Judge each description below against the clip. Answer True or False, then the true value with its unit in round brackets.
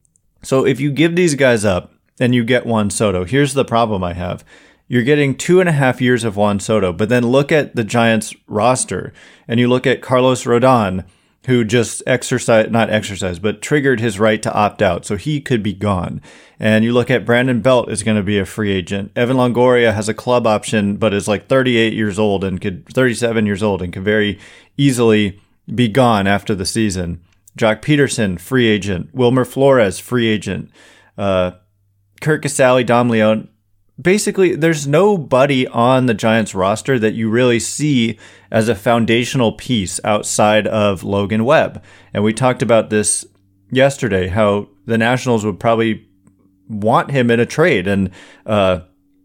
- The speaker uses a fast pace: False (180 wpm)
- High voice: False (110 Hz)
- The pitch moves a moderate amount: True (3.7 semitones)